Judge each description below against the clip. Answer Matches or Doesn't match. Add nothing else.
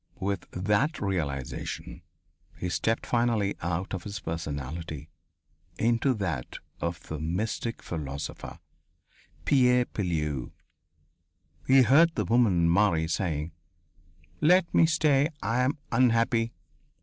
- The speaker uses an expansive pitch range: Matches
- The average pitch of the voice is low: Matches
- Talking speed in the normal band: Doesn't match